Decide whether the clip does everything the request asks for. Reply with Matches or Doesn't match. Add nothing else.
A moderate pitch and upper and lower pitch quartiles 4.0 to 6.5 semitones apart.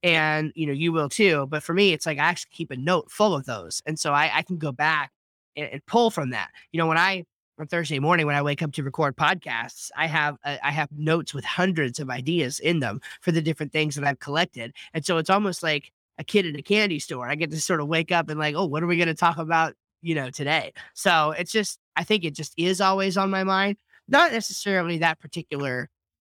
Doesn't match